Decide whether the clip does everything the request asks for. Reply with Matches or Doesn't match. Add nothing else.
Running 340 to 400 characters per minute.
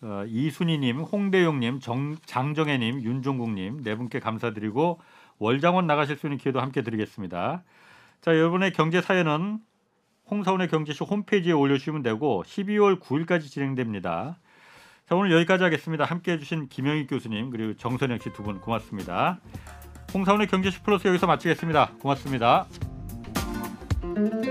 Matches